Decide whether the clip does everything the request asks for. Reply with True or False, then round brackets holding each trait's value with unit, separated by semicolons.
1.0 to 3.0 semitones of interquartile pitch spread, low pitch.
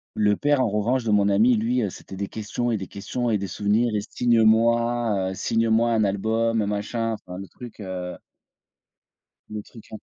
True (2.5 semitones; 110 Hz)